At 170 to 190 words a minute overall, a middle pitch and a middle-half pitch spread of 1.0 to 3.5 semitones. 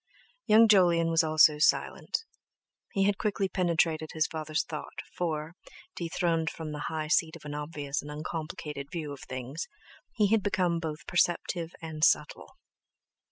No: average, 150 wpm; medium, 160 Hz; narrow, 2.5 semitones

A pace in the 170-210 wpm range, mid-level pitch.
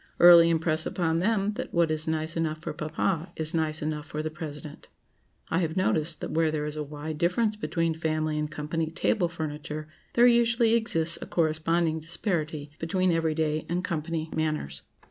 Yes: average, 180 wpm; medium, 160 Hz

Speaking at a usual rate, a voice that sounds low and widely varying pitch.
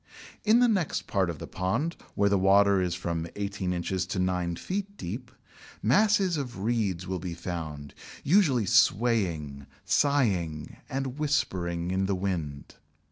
Yes: average, 145 wpm; very low, 95 Hz; wide, 7.1 semitones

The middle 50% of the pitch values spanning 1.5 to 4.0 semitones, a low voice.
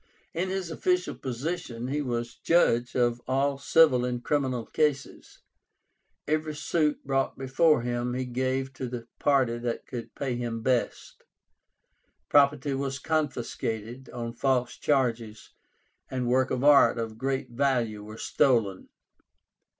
Yes: average, 2.9 semitones; low, 130 Hz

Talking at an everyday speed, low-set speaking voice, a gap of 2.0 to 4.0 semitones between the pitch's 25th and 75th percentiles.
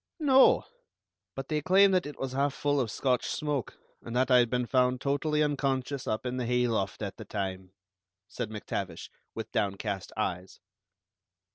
No: average, 165 wpm; low, 125 Hz; average, 4.5 semitones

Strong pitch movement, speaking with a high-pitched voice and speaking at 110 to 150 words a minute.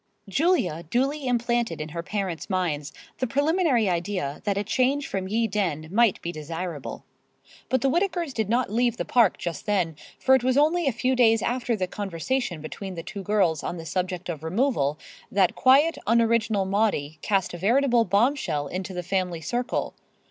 No: wide, 6.1 semitones; high, 205 Hz; average, 175 wpm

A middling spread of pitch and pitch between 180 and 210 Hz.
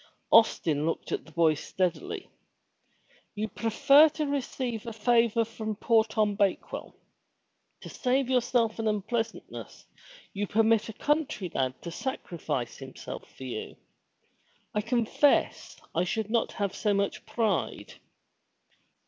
No: average, 3.7 semitones; high, 220 Hz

